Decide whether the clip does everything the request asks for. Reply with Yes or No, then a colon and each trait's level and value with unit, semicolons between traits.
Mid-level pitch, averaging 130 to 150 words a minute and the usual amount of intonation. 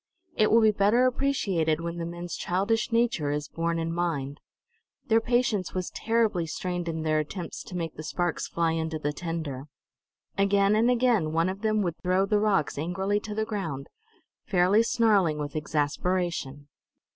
No: medium, 180 Hz; average, 170 wpm; average, 4.8 semitones